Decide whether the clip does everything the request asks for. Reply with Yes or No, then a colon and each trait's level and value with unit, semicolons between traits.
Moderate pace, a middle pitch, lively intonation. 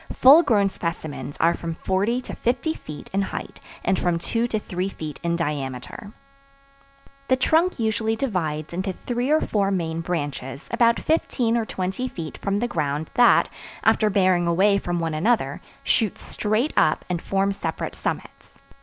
No: average, 165 wpm; high, 195 Hz; wide, 5.7 semitones